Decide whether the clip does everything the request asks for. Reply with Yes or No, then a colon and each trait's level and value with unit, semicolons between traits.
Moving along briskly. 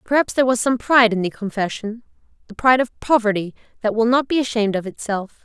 Yes: fast, 210 wpm